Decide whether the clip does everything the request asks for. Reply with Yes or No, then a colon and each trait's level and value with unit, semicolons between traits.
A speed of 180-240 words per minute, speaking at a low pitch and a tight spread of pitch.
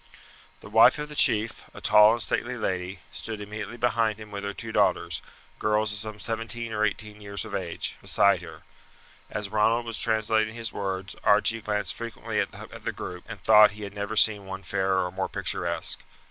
Yes: average, 190 wpm; low, 105 Hz; narrow, 1.8 semitones